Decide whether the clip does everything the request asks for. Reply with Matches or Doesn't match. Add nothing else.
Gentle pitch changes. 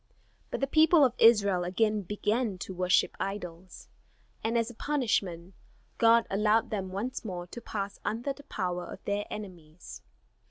Doesn't match